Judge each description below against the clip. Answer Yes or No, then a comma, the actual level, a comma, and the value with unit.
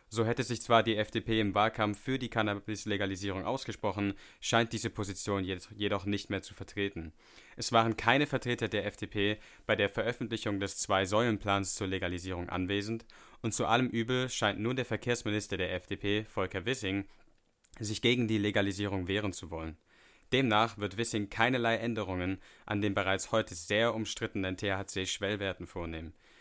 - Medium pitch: No, low, 105 Hz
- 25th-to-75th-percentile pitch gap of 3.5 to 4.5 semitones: No, average, 2.7 semitones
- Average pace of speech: Yes, average, 150 wpm